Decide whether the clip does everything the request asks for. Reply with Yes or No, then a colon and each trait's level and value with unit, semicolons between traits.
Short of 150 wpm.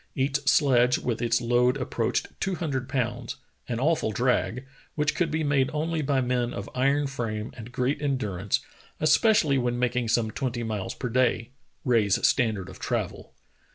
No: average, 170 wpm